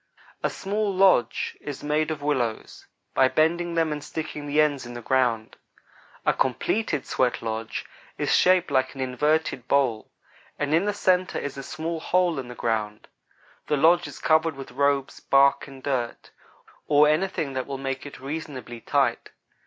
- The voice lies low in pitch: No, medium, 145 Hz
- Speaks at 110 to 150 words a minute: No, average, 165 wpm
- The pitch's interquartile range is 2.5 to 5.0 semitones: Yes, average, 3.6 semitones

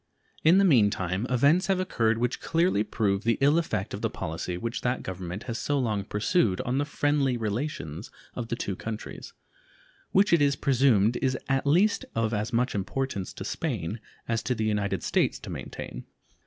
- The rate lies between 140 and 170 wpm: No, average, 185 wpm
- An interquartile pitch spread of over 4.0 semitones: Yes, wide, 5.4 semitones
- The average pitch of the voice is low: Yes, low, 115 Hz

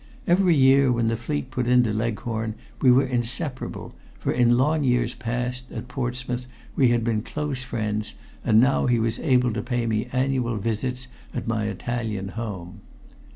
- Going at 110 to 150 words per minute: No, average, 165 wpm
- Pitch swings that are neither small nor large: No, narrow, 2.2 semitones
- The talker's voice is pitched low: Yes, low, 120 Hz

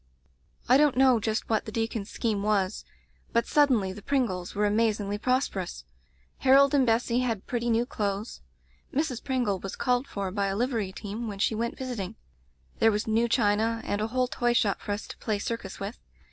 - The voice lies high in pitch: Yes, high, 225 Hz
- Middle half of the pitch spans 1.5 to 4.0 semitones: Yes, average, 3.3 semitones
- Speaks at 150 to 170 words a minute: No, average, 190 wpm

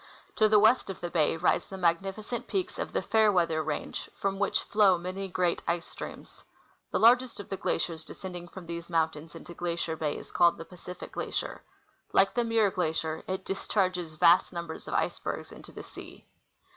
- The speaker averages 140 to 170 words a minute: No, average, 185 wpm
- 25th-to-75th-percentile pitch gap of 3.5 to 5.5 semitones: No, average, 2.9 semitones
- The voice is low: No, medium, 180 Hz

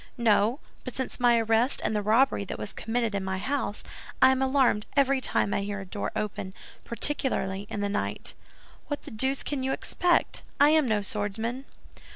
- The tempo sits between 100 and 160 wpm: No, average, 190 wpm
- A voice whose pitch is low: No, high, 230 Hz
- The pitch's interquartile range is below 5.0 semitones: Yes, average, 4.5 semitones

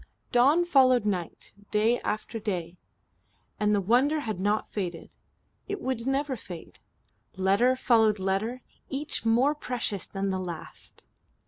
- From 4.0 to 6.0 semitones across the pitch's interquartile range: Yes, average, 4.9 semitones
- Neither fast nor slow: No, slow, 130 wpm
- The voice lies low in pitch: No, high, 225 Hz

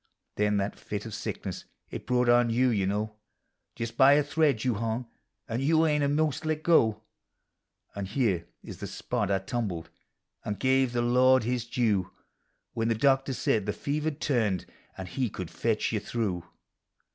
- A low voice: Yes, low, 120 Hz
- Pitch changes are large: No, average, 4.3 semitones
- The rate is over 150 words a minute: Yes, average, 180 wpm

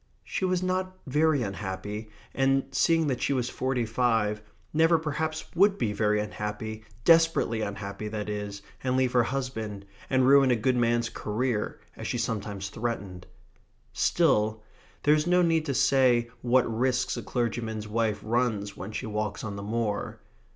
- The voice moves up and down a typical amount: Yes, average, 4.3 semitones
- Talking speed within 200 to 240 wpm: No, average, 160 wpm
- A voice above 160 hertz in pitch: No, low, 120 Hz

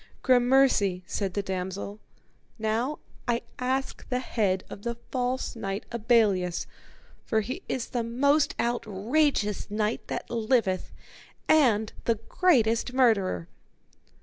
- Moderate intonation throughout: Yes, average, 3.8 semitones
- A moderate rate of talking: No, slow, 115 wpm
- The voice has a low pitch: No, high, 230 Hz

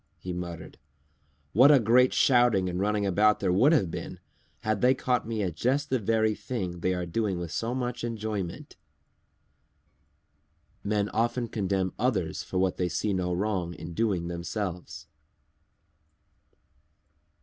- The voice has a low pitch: Yes, low, 105 Hz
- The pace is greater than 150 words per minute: No, average, 145 wpm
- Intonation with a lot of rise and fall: No, average, 4.4 semitones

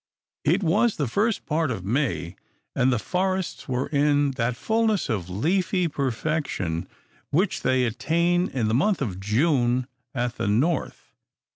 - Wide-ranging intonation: Yes, wide, 6.8 semitones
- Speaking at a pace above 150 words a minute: No, average, 145 wpm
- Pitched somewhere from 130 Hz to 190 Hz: Yes, medium, 140 Hz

